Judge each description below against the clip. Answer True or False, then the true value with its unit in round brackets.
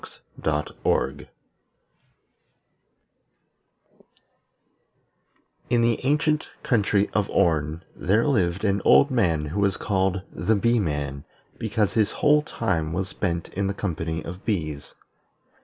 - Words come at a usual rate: False (105 wpm)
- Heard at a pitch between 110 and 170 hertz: False (100 Hz)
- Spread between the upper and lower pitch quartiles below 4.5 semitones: False (5.0 semitones)